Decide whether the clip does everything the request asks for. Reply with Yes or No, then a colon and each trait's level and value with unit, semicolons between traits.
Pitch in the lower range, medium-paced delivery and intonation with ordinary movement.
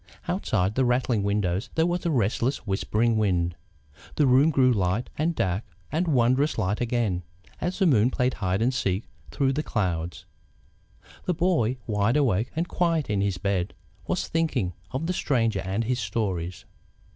No: low, 115 Hz; average, 165 wpm; wide, 6.1 semitones